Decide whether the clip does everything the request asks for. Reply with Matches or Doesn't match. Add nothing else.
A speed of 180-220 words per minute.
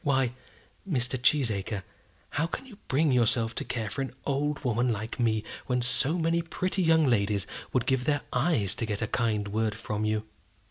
Matches